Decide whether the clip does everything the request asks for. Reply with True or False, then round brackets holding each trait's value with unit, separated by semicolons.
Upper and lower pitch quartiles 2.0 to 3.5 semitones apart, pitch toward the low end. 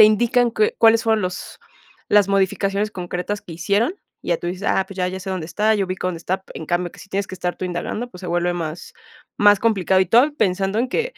False (3.1 semitones; 195 Hz)